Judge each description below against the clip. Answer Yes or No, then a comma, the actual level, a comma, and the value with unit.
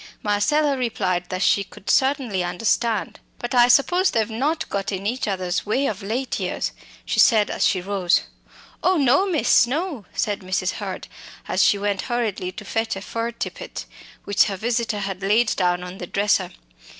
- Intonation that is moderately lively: Yes, average, 4.2 semitones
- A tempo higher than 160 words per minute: Yes, average, 185 wpm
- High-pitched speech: Yes, high, 215 Hz